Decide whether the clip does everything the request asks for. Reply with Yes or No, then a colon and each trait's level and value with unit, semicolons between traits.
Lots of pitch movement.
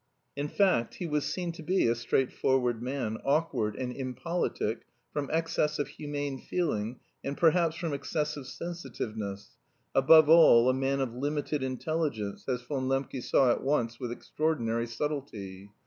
No: average, 4.2 semitones